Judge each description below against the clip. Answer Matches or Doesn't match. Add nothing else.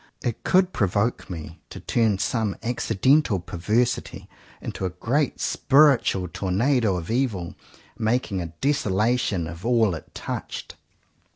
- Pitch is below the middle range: Matches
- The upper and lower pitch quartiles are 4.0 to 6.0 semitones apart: Matches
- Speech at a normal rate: Doesn't match